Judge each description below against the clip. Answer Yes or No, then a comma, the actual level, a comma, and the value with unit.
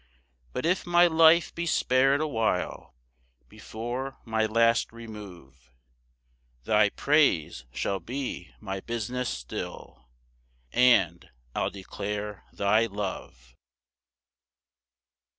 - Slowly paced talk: Yes, slow, 95 wpm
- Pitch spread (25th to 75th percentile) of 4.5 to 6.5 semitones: Yes, wide, 5.4 semitones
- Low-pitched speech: Yes, low, 110 Hz